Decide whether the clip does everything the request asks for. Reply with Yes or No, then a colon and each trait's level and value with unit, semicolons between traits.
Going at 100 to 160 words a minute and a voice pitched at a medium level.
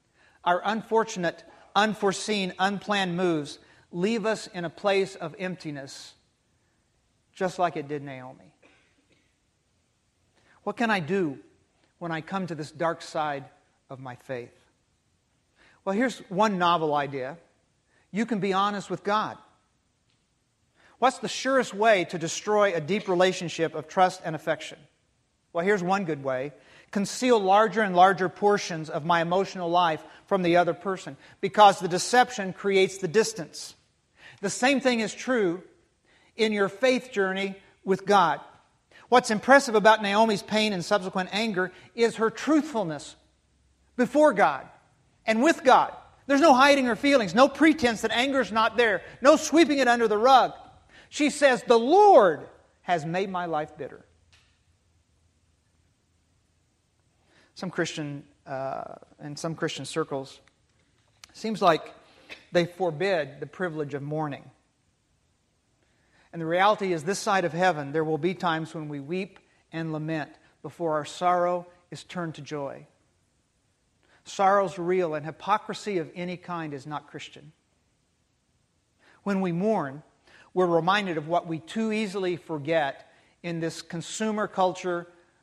Yes: average, 140 wpm; medium, 180 Hz